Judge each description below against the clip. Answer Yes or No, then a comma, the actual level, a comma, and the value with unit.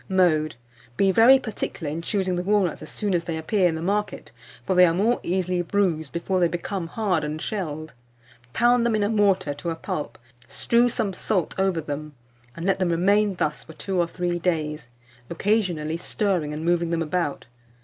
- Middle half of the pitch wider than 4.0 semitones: No, average, 3.7 semitones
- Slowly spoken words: No, average, 190 wpm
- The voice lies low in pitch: No, medium, 180 Hz